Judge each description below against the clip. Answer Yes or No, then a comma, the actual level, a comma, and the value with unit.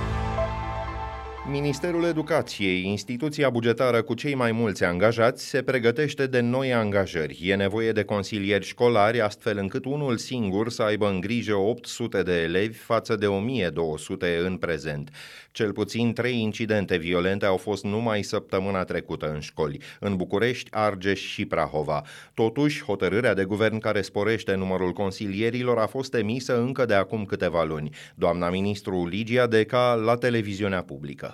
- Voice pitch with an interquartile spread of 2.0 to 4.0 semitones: Yes, average, 3.7 semitones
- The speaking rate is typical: Yes, average, 145 wpm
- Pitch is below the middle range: Yes, low, 110 Hz